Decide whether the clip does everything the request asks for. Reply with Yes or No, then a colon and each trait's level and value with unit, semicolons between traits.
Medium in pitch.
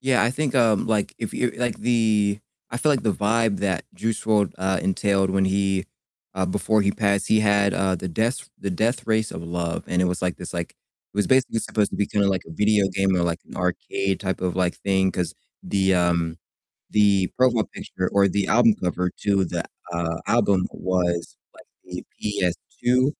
No: low, 100 Hz